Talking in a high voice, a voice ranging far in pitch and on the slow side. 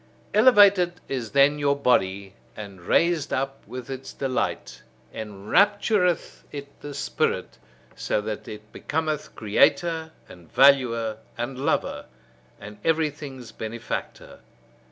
No: low, 135 Hz; wide, 6.3 semitones; slow, 110 wpm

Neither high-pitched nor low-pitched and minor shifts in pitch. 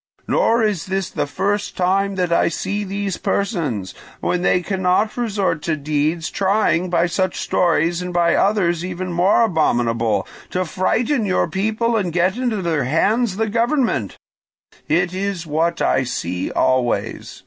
No: medium, 180 Hz; average, 3.5 semitones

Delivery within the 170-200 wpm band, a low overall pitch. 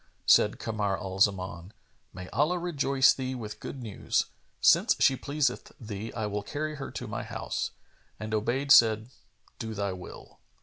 No: average, 160 wpm; low, 110 Hz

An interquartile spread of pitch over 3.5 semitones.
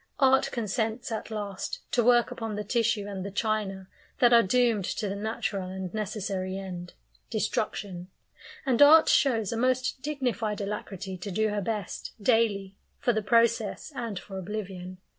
No: average, 3.2 semitones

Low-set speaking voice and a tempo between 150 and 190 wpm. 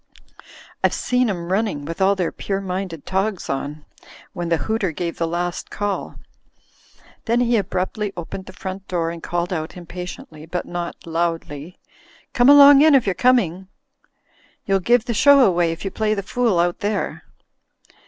No: medium, 185 Hz; average, 165 wpm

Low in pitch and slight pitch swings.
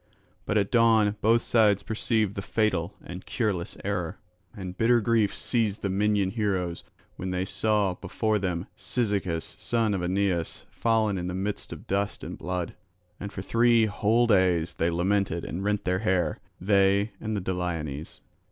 No: low, 100 Hz; average, 3.0 semitones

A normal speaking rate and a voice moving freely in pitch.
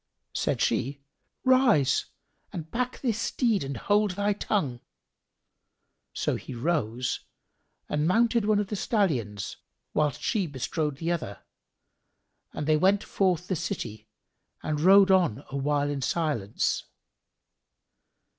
No: slow, 120 wpm; wide, 6.6 semitones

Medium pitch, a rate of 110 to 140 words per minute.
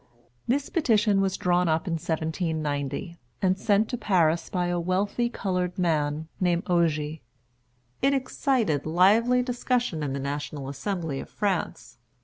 Yes: medium, 180 Hz; slow, 135 wpm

